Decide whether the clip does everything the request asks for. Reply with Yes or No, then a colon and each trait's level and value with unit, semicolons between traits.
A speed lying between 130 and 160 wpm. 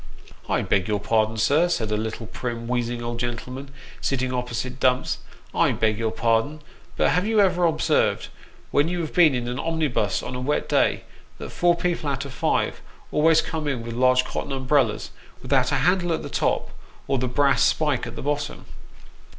No: average, 200 wpm